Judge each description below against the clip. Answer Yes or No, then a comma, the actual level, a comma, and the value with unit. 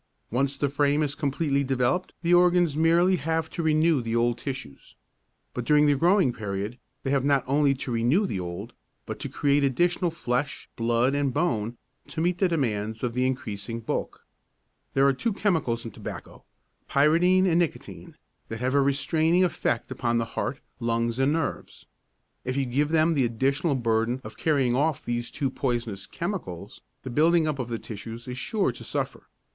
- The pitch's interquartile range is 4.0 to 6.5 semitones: Yes, average, 5.1 semitones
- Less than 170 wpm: No, average, 180 wpm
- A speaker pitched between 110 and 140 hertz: Yes, low, 135 Hz